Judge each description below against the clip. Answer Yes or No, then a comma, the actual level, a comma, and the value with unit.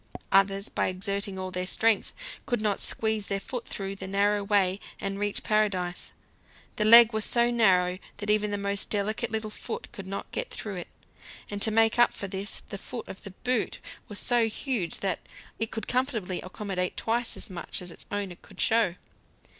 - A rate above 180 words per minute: Yes, average, 190 wpm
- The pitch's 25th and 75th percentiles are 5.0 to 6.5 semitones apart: No, narrow, 2.5 semitones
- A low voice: No, high, 205 Hz